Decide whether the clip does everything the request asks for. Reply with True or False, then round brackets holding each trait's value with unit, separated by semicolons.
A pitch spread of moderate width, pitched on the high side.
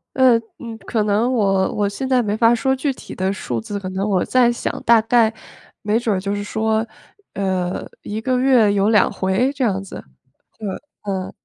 True (3.3 semitones; 215 Hz)